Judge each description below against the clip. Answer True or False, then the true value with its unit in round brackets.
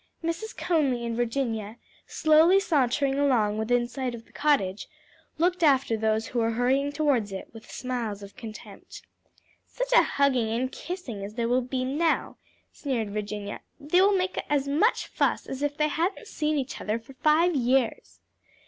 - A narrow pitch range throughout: False (5.1 semitones)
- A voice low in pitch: False (260 Hz)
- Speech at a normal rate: True (165 wpm)